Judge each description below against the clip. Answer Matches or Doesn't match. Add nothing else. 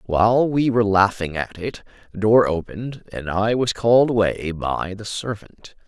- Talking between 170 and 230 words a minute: Matches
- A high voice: Doesn't match